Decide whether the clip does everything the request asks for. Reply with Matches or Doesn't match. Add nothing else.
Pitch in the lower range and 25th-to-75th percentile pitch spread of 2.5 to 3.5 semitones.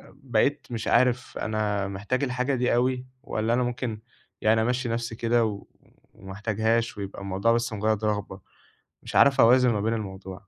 Matches